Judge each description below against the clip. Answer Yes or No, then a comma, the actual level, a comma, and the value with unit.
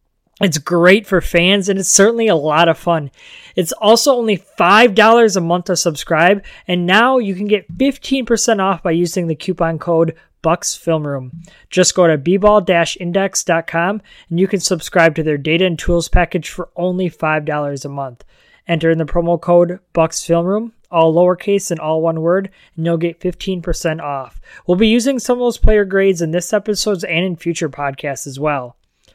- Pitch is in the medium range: Yes, medium, 175 Hz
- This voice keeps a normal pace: Yes, average, 175 wpm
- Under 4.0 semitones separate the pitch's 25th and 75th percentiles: Yes, average, 3.4 semitones